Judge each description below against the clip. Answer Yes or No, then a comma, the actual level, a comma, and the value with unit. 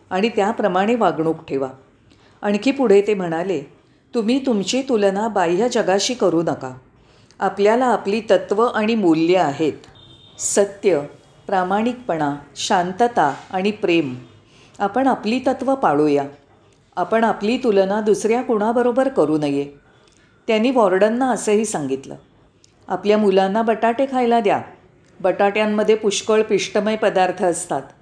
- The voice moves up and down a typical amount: No, wide, 5.9 semitones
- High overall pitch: Yes, high, 200 Hz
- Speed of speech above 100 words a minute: Yes, average, 110 wpm